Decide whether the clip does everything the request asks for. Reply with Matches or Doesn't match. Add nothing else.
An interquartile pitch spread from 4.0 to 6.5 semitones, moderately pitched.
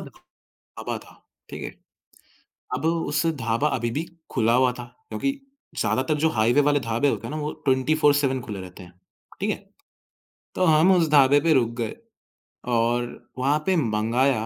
Doesn't match